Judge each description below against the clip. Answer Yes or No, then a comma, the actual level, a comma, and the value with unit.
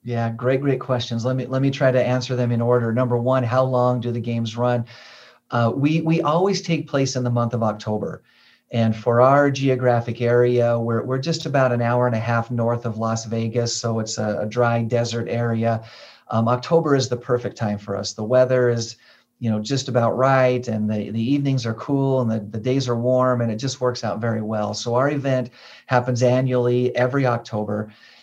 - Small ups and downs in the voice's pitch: Yes, narrow, 1.9 semitones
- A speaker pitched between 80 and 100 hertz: No, low, 120 Hz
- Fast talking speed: Yes, fast, 215 wpm